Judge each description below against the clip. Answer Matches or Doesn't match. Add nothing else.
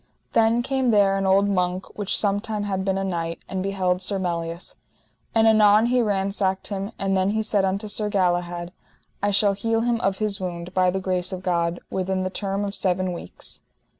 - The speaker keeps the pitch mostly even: Matches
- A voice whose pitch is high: Matches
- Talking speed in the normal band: Matches